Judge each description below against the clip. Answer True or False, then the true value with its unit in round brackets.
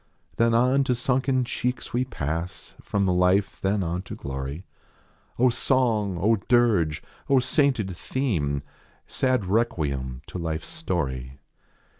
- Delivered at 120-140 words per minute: True (135 wpm)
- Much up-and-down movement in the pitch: True (7.4 semitones)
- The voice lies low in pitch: True (100 Hz)